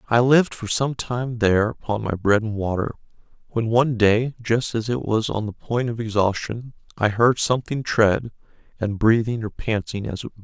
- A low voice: Yes, low, 115 Hz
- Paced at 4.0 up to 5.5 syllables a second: Yes, 5.2 syllables/s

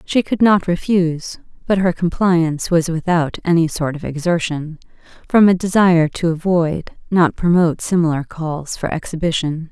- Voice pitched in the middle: Yes, medium, 170 Hz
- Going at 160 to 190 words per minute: No, average, 150 wpm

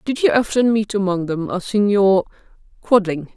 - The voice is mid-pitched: No, high, 200 Hz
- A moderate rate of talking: Yes, average, 145 wpm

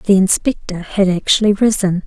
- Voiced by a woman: Yes, female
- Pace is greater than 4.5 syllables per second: Yes, 4.9 syllables/s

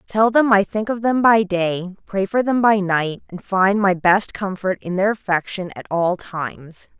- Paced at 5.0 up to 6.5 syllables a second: No, 4.5 syllables/s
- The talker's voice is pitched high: Yes, high, 195 Hz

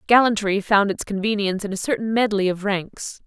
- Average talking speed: Yes, average, 185 wpm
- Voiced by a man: No, female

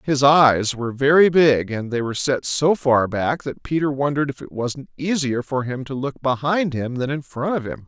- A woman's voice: No, male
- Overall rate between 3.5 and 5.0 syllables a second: Yes, 4.9 syllables/s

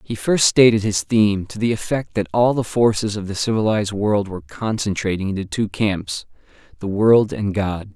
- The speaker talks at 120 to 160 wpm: No, average, 180 wpm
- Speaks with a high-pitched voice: No, low, 105 Hz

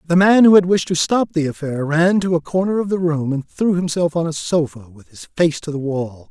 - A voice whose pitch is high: No, medium, 165 Hz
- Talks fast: Yes, fast, 265 wpm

